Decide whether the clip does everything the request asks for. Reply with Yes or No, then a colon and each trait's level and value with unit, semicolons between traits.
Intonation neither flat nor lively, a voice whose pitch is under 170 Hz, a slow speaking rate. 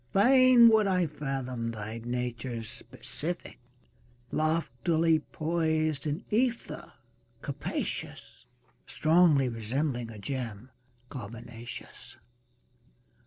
No: wide, 5.8 semitones; medium, 140 Hz; slow, 75 wpm